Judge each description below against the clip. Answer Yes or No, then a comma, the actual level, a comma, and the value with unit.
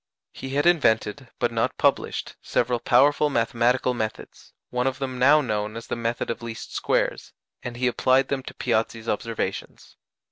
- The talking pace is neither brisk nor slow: Yes, average, 165 wpm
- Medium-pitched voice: No, low, 125 Hz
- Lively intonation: No, narrow, 2.6 semitones